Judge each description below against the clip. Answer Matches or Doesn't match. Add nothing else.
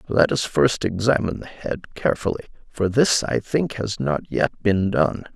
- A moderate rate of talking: Matches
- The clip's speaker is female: Doesn't match